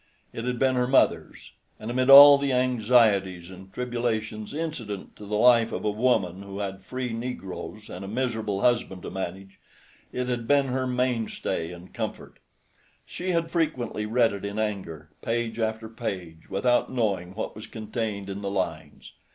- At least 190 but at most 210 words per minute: No, average, 170 wpm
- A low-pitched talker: Yes, low, 110 Hz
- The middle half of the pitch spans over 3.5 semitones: Yes, average, 4.2 semitones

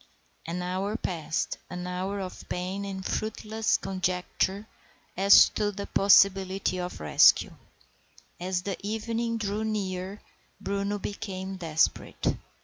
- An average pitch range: No, narrow, 2.0 semitones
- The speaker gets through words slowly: Yes, slow, 115 wpm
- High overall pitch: Yes, high, 195 Hz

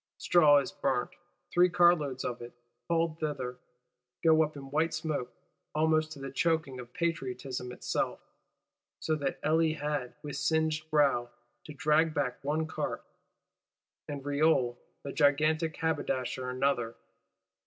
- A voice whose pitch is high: No, medium, 150 Hz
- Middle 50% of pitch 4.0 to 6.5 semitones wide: No, average, 2.9 semitones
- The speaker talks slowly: Yes, slow, 130 wpm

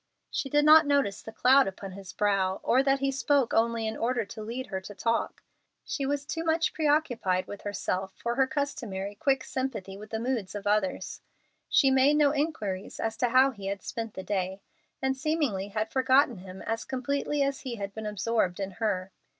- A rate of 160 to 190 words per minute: No, average, 200 wpm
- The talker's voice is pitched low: No, high, 230 Hz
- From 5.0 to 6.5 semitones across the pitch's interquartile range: Yes, wide, 5.5 semitones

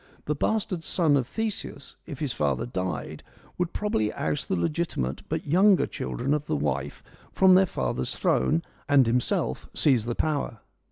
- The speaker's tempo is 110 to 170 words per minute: Yes, average, 160 wpm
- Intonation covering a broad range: Yes, wide, 8.0 semitones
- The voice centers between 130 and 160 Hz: Yes, medium, 140 Hz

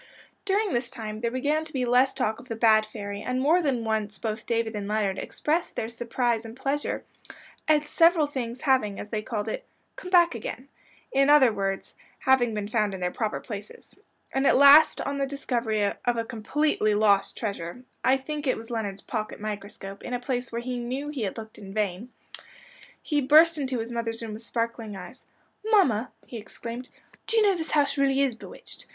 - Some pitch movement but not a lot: Yes, average, 4.3 semitones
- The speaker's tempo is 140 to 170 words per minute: No, average, 200 wpm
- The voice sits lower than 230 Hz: No, high, 235 Hz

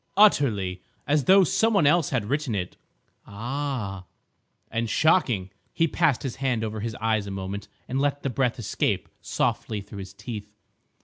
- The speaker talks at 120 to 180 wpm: Yes, average, 165 wpm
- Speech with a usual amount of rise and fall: No, wide, 5.9 semitones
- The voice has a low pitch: Yes, low, 120 Hz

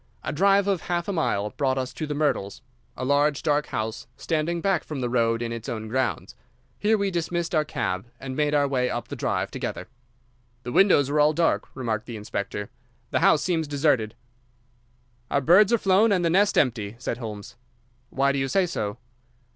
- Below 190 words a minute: No, average, 195 wpm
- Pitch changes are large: Yes, wide, 6.3 semitones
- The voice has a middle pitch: Yes, medium, 145 Hz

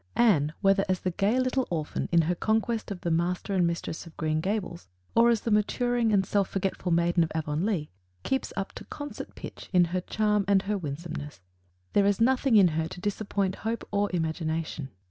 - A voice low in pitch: No, high, 190 Hz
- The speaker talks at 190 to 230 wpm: Yes, average, 195 wpm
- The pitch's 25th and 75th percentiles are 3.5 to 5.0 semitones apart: Yes, average, 4.0 semitones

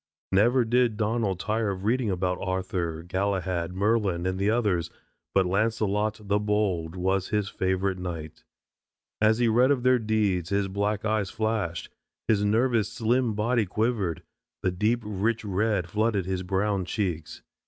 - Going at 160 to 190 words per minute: No, average, 150 wpm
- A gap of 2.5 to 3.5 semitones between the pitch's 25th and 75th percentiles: Yes, average, 3.0 semitones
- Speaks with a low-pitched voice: Yes, low, 105 Hz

